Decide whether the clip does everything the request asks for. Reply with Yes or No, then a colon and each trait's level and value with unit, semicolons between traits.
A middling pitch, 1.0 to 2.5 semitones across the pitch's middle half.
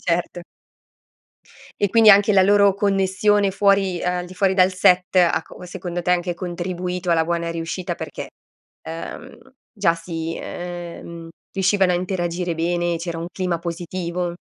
Yes: medium, 180 Hz; narrow, 1.9 semitones